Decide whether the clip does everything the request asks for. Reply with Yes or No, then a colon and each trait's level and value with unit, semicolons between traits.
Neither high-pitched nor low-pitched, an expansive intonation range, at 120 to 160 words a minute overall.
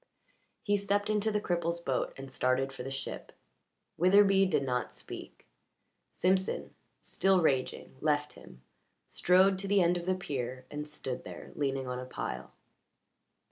Yes: medium, 170 Hz; wide, 6.2 semitones; average, 150 wpm